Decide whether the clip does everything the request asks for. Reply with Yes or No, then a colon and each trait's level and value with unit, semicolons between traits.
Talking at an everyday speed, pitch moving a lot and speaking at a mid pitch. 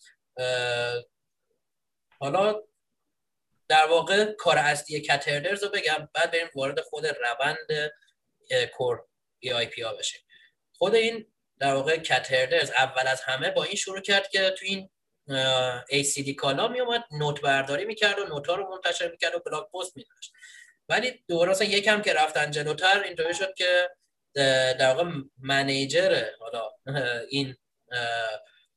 Yes: average, 135 wpm; wide, 6.7 semitones; medium, 165 Hz